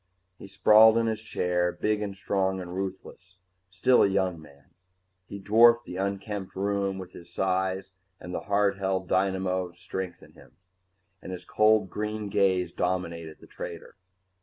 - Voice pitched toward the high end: No, very low, 95 Hz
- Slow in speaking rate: No, average, 160 wpm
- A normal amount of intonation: No, narrow, 1.9 semitones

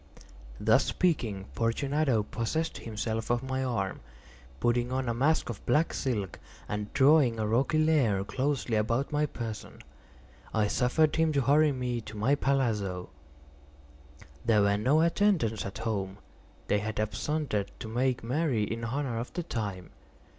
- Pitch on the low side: Yes, low, 120 Hz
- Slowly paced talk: No, average, 145 wpm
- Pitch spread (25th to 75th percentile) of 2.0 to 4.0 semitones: No, average, 4.7 semitones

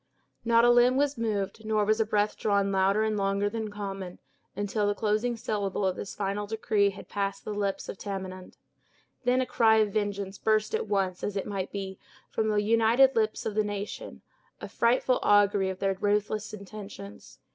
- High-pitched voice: Yes, high, 205 Hz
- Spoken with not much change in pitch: Yes, narrow, 1.7 semitones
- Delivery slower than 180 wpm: No, average, 190 wpm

